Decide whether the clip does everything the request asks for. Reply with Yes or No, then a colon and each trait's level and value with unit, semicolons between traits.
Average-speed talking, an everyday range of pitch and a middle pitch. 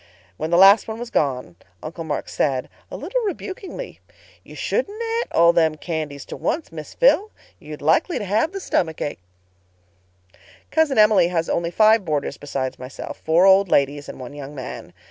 No: average, 165 wpm; wide, 8.7 semitones; medium, 170 Hz